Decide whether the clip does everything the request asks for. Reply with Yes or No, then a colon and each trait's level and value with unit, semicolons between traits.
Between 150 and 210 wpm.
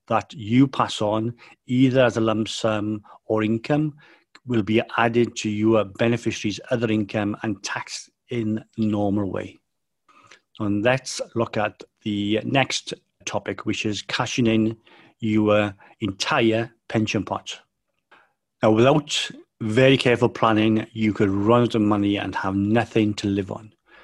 No: average, 140 wpm